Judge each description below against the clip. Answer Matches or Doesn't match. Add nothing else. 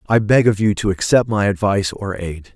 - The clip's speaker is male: Matches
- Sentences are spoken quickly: Matches